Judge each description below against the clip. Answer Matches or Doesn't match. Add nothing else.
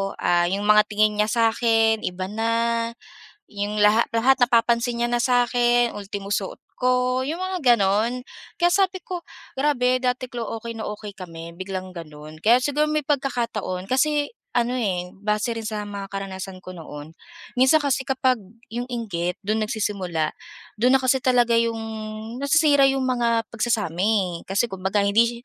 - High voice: Matches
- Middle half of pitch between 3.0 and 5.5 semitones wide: Matches